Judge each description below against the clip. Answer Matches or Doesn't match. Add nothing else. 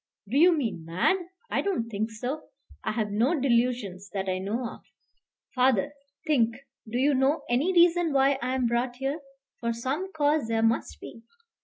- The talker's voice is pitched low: Doesn't match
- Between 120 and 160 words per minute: Doesn't match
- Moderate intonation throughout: Matches